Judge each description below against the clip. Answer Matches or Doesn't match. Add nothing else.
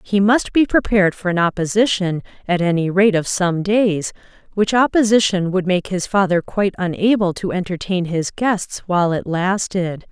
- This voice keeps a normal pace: Matches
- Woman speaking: Matches